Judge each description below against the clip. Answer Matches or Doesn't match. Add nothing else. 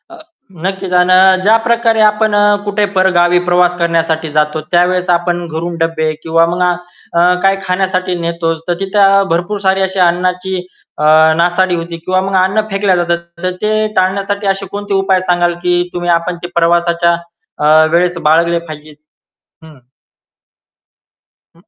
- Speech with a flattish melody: Matches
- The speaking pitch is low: Doesn't match